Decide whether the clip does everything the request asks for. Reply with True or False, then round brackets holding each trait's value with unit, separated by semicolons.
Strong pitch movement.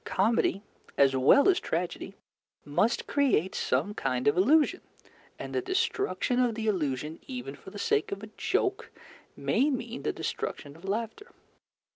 True (8.6 semitones)